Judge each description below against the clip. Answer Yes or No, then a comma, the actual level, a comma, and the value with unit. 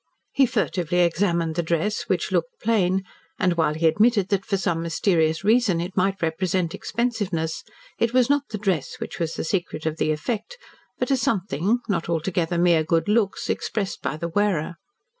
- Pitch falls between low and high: Yes, medium, 180 Hz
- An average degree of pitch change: Yes, average, 4.2 semitones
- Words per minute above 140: Yes, average, 180 wpm